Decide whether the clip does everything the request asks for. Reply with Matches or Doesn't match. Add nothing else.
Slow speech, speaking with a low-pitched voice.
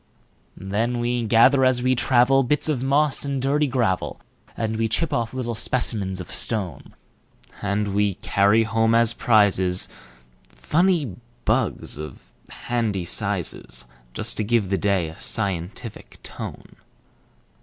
Matches